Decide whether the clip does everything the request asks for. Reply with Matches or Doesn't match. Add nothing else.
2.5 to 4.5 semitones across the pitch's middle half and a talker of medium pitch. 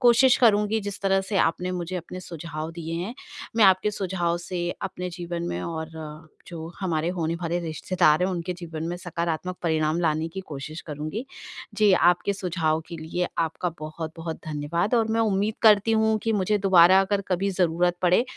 Matches